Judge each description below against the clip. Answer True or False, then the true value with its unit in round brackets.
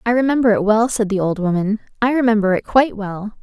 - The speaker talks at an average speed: False (230 wpm)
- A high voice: True (220 Hz)